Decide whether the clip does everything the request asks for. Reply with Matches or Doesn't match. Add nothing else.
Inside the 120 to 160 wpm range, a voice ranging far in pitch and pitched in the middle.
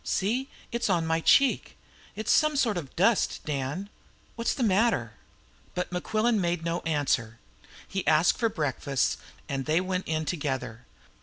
Matches